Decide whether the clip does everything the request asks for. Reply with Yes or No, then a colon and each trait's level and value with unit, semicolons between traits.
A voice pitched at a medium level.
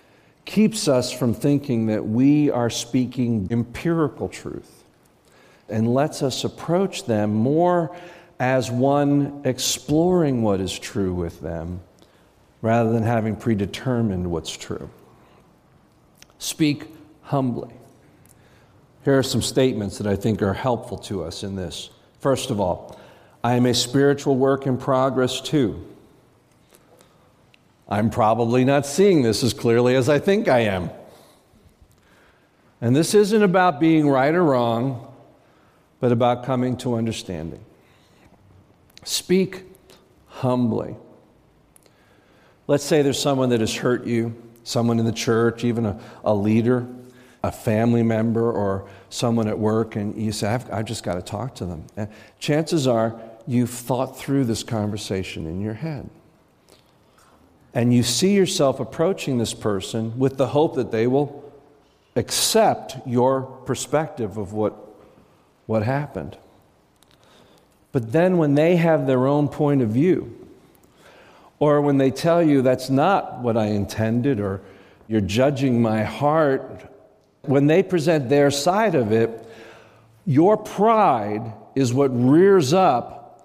No: low, 125 Hz